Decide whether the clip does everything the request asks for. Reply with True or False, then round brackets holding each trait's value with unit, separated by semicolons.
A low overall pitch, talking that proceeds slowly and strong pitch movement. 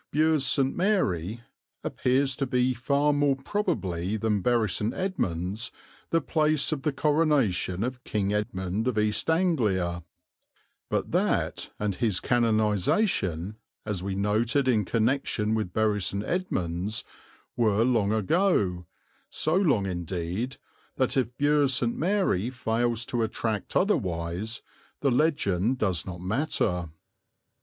True (115 Hz; 125 wpm; 6.1 semitones)